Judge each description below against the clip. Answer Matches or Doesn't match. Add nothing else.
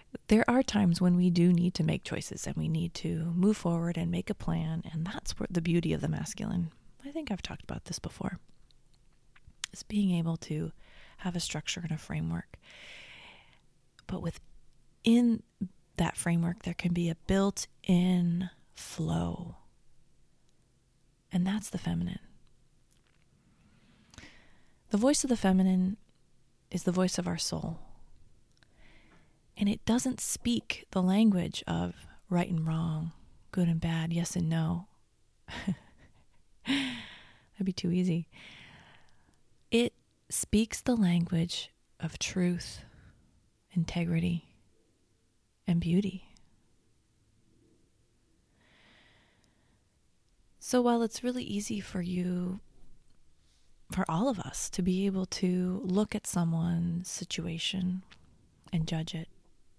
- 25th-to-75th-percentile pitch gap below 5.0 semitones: Doesn't match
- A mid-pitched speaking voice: Matches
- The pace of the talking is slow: Matches